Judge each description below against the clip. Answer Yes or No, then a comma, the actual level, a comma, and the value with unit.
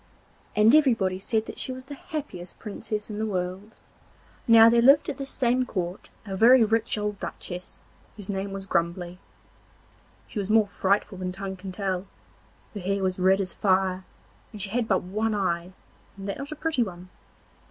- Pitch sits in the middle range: No, high, 200 Hz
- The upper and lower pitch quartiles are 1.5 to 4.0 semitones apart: Yes, average, 3.3 semitones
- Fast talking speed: No, average, 175 wpm